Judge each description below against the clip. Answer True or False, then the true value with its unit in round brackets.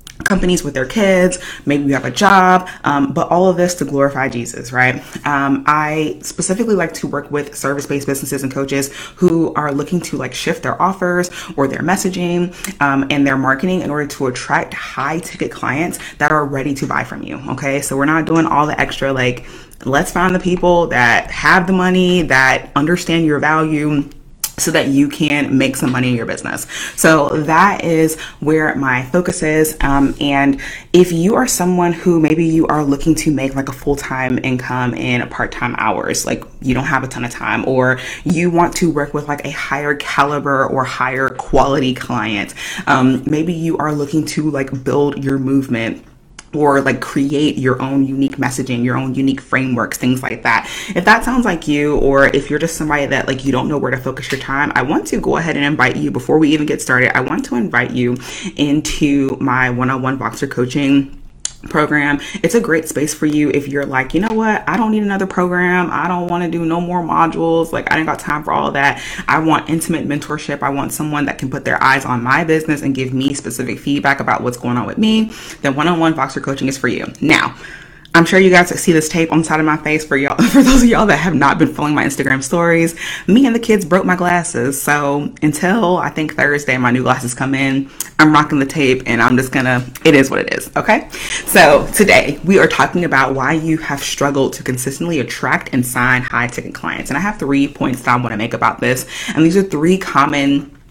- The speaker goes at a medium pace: False (220 wpm)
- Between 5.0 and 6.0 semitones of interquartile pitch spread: False (3.7 semitones)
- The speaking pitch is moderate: True (145 Hz)